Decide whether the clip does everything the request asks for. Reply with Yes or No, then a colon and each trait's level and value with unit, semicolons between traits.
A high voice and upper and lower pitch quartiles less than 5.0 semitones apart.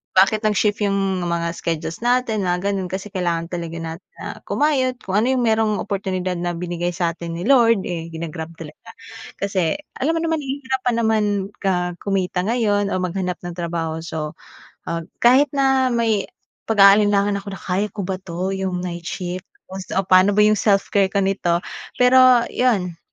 Yes: high, 195 Hz; average, 3.9 semitones